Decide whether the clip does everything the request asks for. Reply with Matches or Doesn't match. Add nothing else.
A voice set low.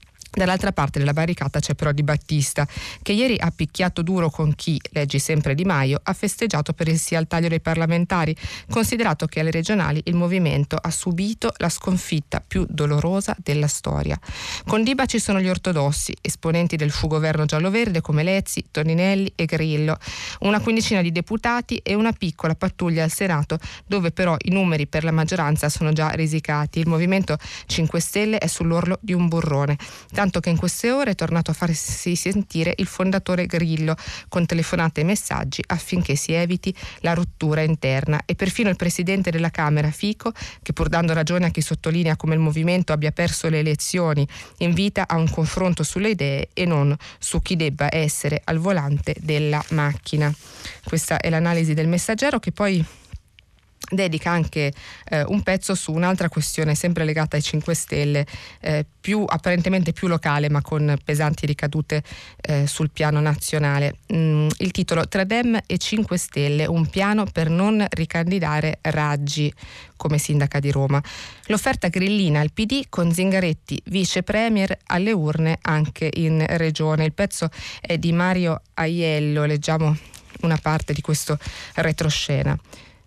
Doesn't match